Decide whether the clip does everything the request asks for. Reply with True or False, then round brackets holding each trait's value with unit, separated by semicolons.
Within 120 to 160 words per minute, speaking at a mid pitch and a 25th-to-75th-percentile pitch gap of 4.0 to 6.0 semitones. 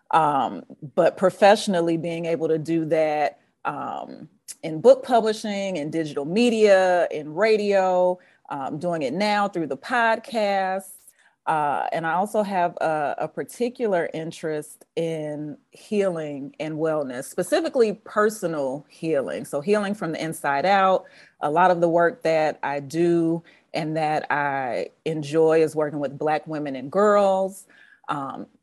True (140 wpm; 170 Hz; 4.6 semitones)